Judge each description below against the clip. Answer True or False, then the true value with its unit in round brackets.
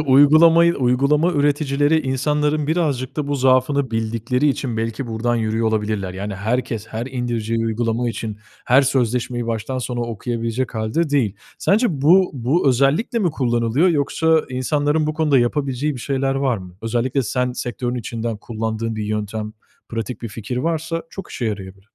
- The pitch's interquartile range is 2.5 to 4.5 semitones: True (4.2 semitones)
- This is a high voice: False (125 Hz)